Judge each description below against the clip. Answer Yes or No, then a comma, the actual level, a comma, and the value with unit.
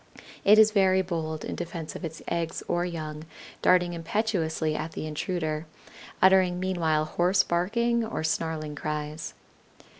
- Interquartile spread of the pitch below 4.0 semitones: Yes, average, 3.1 semitones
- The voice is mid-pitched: Yes, medium, 170 Hz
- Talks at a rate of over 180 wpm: No, average, 140 wpm